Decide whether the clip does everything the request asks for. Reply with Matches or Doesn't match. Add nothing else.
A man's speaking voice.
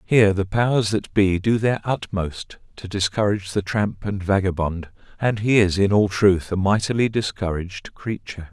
Matches